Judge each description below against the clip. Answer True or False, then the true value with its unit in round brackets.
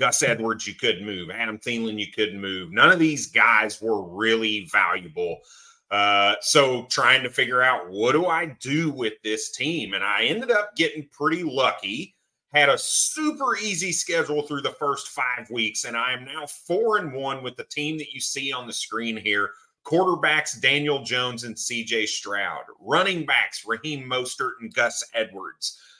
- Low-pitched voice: True (130 Hz)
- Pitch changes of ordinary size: False (5.8 semitones)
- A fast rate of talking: False (180 wpm)